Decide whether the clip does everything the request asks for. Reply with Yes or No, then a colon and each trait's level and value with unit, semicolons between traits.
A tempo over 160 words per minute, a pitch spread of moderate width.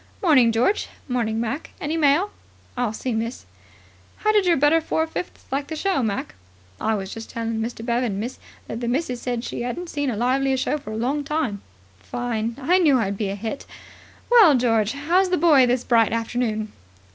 Yes: average, 195 wpm; average, 4.8 semitones